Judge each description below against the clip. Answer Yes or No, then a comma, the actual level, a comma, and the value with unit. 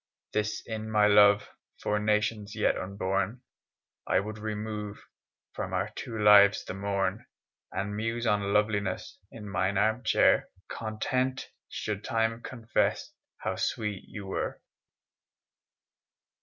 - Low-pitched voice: Yes, low, 105 Hz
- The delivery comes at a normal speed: No, slow, 115 wpm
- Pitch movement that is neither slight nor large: No, narrow, 1.5 semitones